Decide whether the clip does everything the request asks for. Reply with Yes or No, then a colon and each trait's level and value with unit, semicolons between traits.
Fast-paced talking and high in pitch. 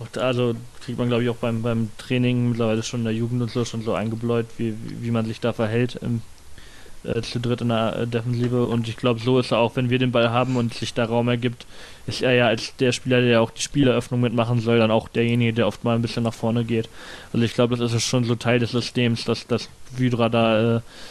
No: fast, 255 wpm; low, 120 Hz